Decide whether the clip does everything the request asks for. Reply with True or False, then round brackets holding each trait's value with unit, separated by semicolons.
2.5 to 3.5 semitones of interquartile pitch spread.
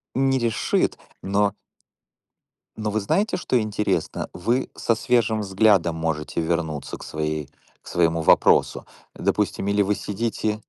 False (4.9 semitones)